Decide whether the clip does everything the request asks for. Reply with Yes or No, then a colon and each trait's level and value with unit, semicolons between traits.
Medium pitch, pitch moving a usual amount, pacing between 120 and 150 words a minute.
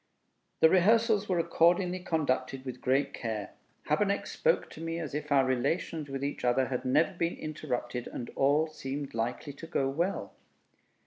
No: medium, 145 Hz; average, 4.3 semitones; average, 165 wpm